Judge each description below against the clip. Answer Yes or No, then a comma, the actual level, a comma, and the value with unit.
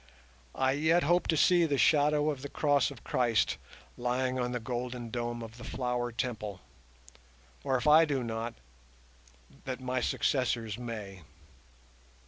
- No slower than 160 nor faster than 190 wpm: No, average, 145 wpm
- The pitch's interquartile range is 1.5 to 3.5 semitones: Yes, average, 3.2 semitones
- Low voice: Yes, low, 125 Hz